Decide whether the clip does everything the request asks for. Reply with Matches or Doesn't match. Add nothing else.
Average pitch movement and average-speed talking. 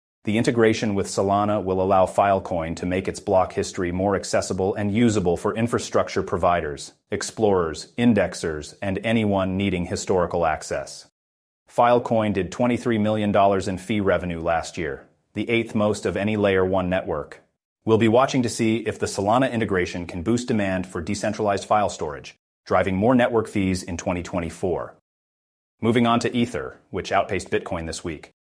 Matches